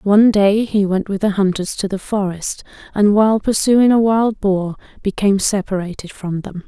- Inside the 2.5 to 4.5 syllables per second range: No, 4.9 syllables/s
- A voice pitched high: Yes, high, 200 Hz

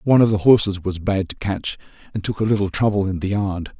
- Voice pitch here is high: No, low, 100 Hz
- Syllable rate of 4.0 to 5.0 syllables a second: No, 6.1 syllables/s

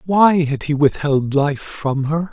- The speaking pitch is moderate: Yes, medium, 150 Hz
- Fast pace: No, average, 180 wpm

